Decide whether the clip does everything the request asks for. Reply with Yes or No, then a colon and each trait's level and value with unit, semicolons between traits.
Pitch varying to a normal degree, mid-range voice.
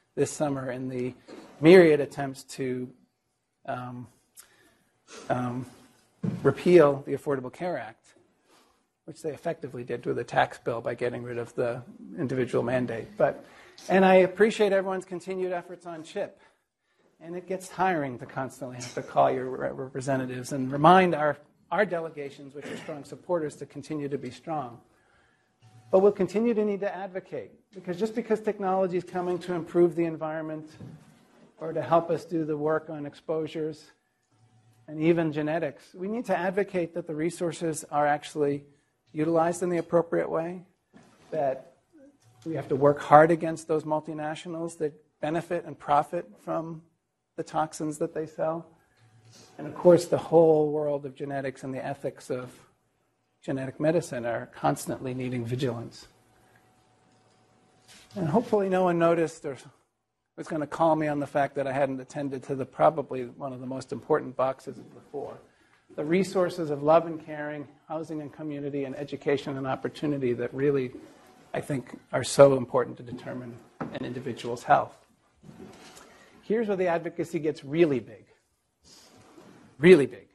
Yes: average, 4.4 semitones; medium, 150 Hz